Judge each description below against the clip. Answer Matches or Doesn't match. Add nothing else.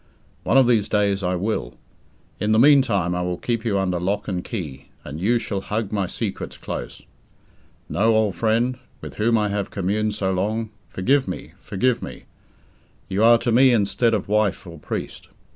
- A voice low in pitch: Matches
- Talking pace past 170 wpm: Matches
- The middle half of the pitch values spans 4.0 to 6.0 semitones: Doesn't match